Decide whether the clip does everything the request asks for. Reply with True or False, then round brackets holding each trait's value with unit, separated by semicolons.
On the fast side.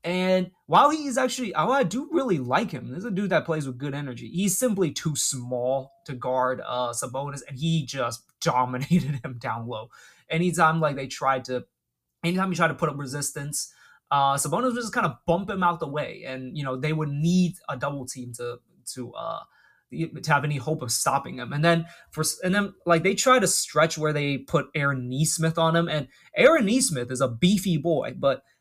True (210 wpm)